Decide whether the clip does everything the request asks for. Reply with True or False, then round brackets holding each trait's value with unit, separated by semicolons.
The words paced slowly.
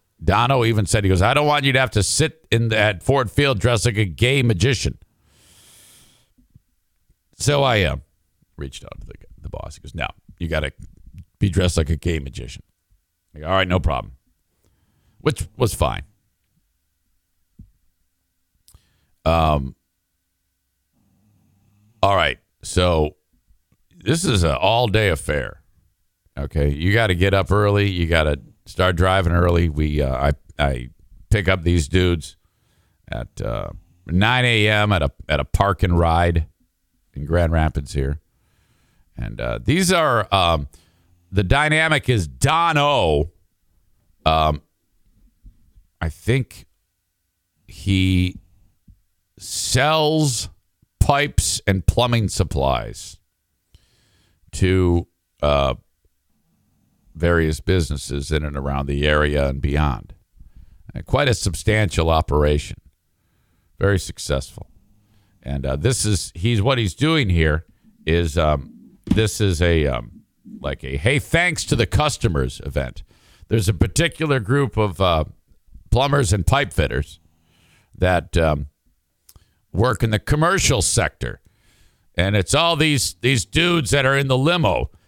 True (130 wpm)